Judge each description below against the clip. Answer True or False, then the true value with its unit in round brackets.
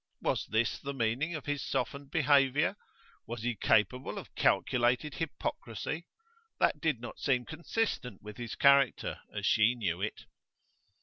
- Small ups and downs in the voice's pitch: False (3.8 semitones)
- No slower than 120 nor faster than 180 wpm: True (140 wpm)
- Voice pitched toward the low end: True (130 Hz)